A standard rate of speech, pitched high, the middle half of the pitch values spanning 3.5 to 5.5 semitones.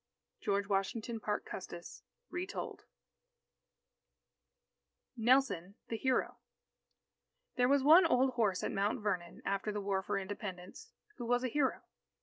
No: slow, 125 wpm; high, 215 Hz; average, 4.5 semitones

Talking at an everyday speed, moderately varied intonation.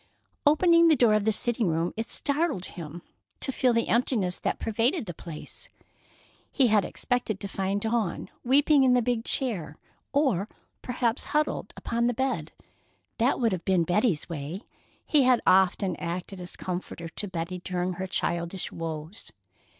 No: average, 160 wpm; wide, 5.8 semitones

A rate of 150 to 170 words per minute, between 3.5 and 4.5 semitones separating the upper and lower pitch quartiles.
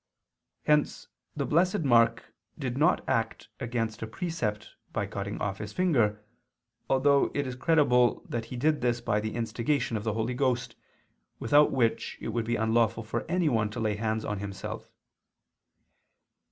Yes: average, 155 wpm; average, 4.1 semitones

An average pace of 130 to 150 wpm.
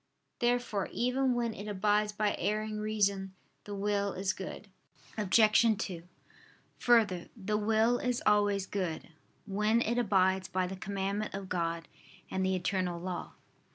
Yes: average, 140 wpm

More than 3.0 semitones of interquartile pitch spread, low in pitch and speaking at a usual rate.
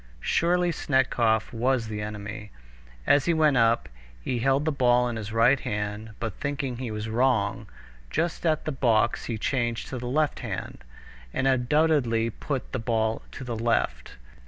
Yes: average, 3.5 semitones; low, 120 Hz; average, 165 wpm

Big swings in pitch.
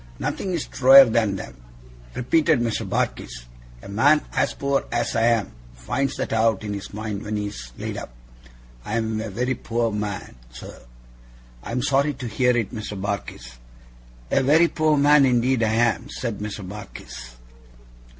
No: average, 4.3 semitones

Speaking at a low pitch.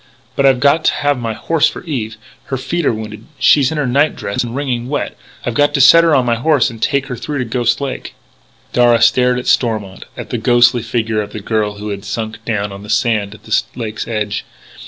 Yes: low, 120 Hz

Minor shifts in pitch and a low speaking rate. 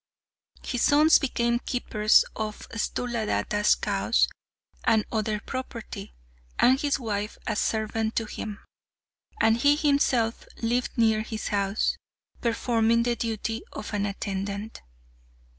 Yes: narrow, 2.1 semitones; slow, 115 wpm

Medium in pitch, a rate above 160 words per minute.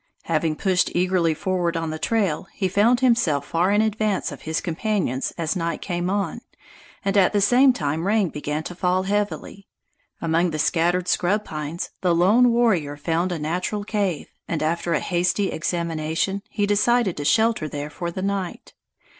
Yes: medium, 180 Hz; average, 170 wpm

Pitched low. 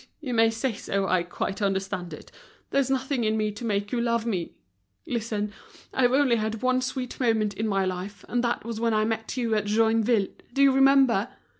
No: high, 225 Hz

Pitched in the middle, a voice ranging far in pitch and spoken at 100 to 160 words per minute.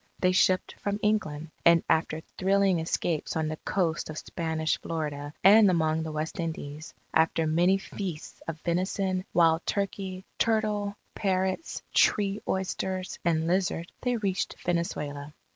No: medium, 175 Hz; average, 3.4 semitones; slow, 135 wpm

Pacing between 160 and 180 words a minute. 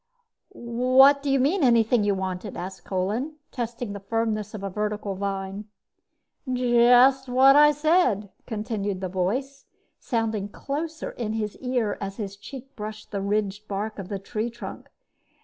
No: average, 150 wpm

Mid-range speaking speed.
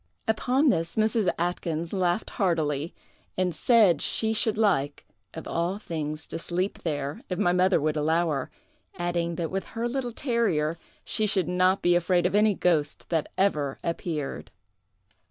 Yes: average, 155 wpm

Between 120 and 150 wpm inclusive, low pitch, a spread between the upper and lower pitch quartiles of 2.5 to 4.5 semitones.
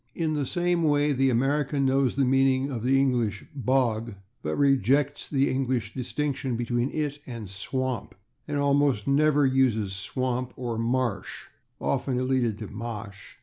Yes: average, 145 wpm; low, 130 Hz; average, 2.9 semitones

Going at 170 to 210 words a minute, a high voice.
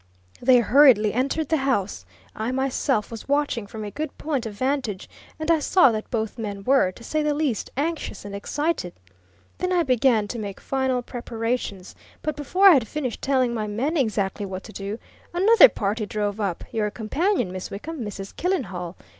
Yes: average, 180 wpm; high, 240 Hz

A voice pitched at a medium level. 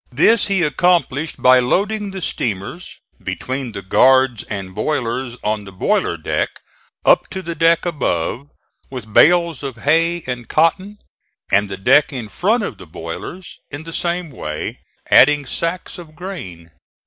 Yes: medium, 145 Hz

